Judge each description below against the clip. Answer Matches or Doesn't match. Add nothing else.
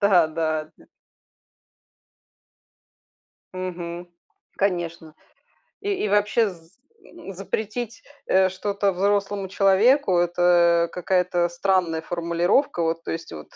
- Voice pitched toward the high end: Doesn't match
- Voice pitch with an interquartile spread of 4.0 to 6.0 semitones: Doesn't match